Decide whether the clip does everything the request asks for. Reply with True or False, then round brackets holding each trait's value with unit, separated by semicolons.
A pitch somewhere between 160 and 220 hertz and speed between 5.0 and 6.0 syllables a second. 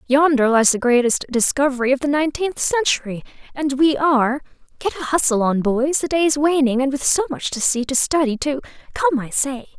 False (270 Hz; 5.5 syllables/s)